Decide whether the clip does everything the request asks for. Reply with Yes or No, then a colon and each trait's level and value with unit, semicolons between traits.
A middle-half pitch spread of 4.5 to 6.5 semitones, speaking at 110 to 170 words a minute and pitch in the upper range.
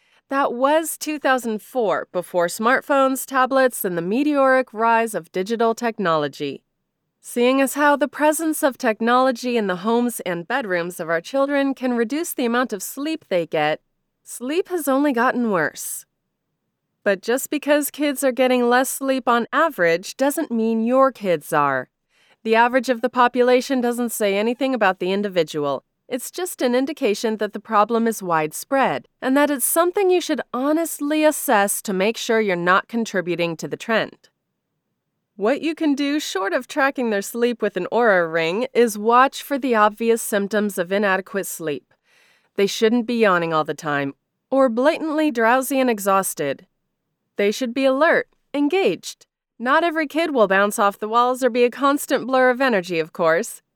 Yes: average, 5.3 semitones; average, 165 wpm; high, 240 Hz